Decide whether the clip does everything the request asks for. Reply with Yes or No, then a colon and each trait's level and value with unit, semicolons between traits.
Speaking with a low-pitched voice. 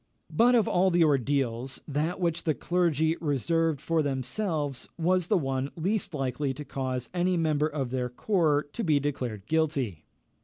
No: medium, 150 Hz